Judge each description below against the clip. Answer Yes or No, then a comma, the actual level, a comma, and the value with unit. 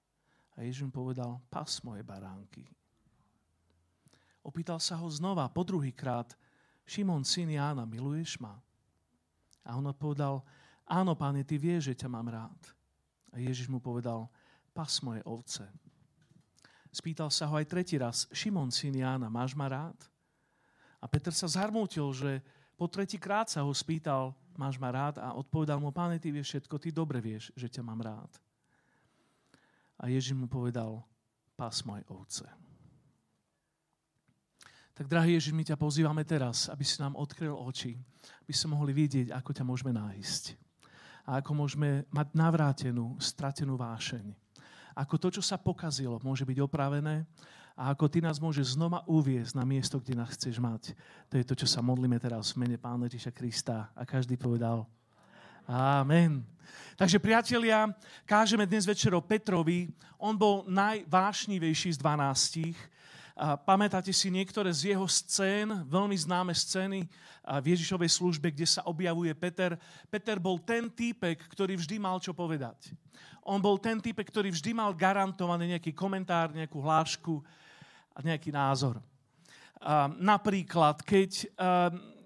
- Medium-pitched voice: Yes, medium, 150 Hz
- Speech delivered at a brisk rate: No, average, 145 wpm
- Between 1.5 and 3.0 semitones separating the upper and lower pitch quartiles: No, wide, 5.4 semitones